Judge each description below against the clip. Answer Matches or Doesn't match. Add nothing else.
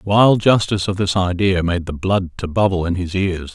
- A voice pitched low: Matches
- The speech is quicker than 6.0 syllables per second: Doesn't match